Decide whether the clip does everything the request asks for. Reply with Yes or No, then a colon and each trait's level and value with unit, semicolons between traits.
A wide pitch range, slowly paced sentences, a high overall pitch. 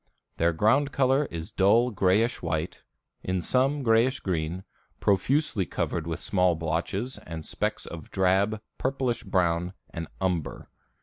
No: wide, 6.3 semitones; slow, 130 wpm; very low, 95 Hz